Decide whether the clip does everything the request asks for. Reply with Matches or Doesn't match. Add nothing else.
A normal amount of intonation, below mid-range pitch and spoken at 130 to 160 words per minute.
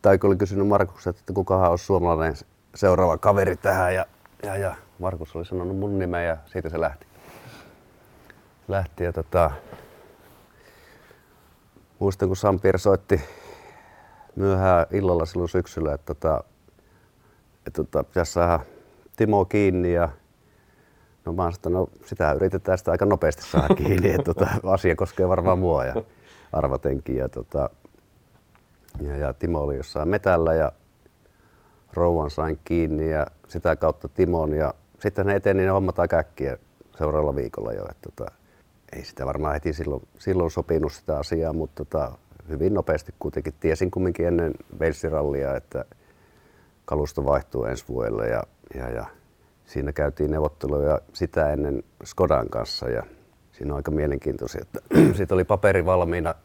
Matches